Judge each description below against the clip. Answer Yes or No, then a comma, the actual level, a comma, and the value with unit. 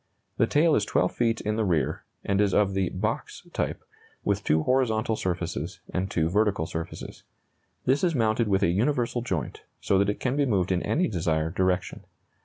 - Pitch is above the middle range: No, low, 100 Hz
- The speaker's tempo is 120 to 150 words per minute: No, average, 190 wpm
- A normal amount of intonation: Yes, average, 4.6 semitones